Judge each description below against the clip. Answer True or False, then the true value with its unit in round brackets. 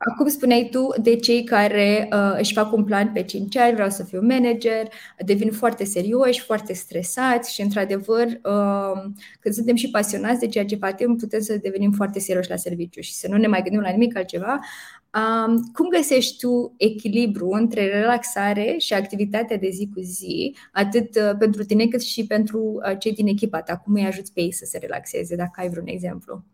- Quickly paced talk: True (190 wpm)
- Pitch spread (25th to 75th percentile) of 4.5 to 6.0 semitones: False (2.9 semitones)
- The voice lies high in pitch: True (215 Hz)